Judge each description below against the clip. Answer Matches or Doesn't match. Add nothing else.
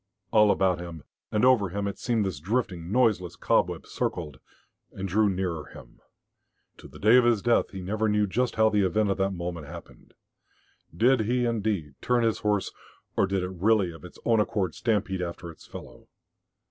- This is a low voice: Matches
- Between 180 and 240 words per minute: Matches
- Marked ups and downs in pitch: Doesn't match